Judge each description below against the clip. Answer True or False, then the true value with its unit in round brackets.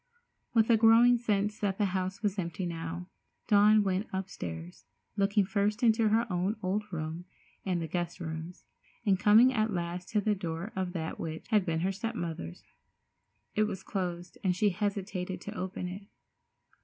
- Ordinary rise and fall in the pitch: True (3.2 semitones)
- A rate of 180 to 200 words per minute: False (170 wpm)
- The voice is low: False (190 Hz)